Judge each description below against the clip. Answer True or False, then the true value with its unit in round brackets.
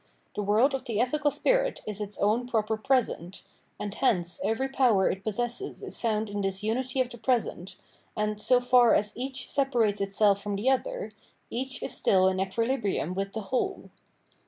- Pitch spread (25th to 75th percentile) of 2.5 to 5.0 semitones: True (4.2 semitones)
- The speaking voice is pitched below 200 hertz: False (220 Hz)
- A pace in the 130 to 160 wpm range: False (180 wpm)